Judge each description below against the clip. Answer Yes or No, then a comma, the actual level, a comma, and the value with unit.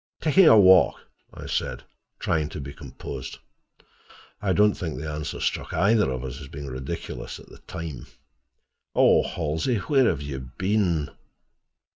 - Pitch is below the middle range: Yes, very low, 80 Hz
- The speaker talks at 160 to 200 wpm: No, average, 150 wpm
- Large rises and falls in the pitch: Yes, wide, 6.3 semitones